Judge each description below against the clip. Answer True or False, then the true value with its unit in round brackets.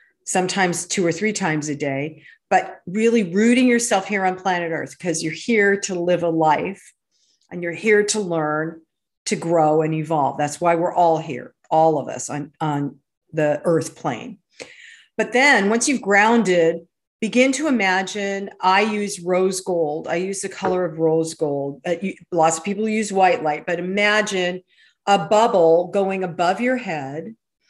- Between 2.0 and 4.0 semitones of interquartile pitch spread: False (4.4 semitones)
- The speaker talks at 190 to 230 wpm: False (170 wpm)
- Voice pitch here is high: False (180 Hz)